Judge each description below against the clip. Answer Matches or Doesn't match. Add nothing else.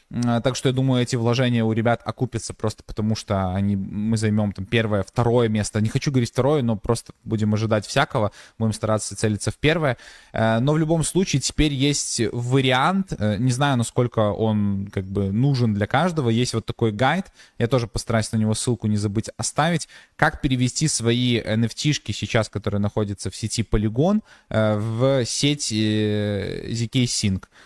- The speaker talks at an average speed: Doesn't match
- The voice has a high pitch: Doesn't match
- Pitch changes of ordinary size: Matches